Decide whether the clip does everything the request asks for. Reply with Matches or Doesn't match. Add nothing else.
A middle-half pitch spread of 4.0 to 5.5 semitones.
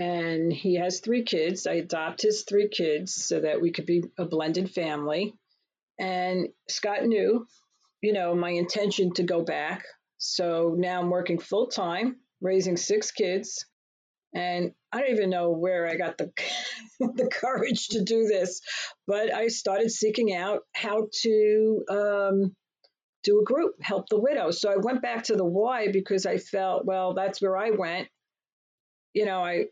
Doesn't match